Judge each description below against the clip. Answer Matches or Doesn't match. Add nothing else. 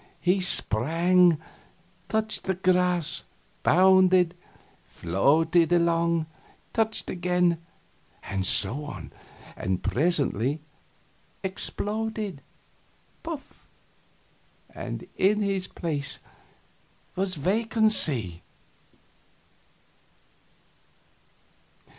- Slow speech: Matches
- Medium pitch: Matches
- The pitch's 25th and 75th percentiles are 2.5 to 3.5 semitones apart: Doesn't match